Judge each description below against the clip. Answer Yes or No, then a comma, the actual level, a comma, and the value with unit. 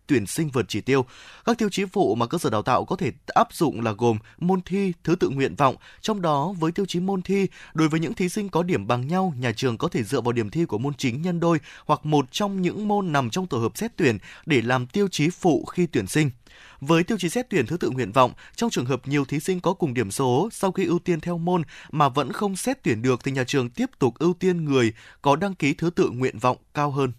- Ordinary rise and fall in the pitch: No, wide, 6.2 semitones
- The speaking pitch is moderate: Yes, medium, 160 Hz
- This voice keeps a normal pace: No, fast, 270 wpm